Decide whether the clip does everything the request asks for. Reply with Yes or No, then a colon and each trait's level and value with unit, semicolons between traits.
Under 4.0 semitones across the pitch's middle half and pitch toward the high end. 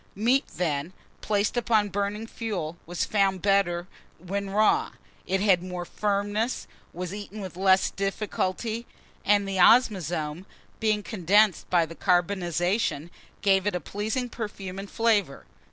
Yes: average, 2.9 semitones; high, 195 Hz